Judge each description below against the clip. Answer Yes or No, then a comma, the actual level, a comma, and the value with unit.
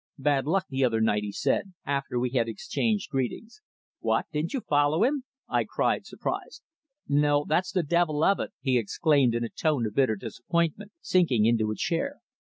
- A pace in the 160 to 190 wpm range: Yes, average, 185 wpm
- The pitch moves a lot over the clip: Yes, wide, 6.2 semitones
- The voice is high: No, medium, 145 Hz